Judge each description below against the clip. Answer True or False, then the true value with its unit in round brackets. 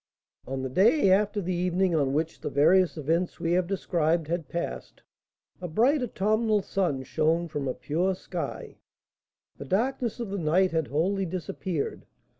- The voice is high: False (175 Hz)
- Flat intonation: False (3.7 semitones)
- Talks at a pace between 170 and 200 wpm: False (160 wpm)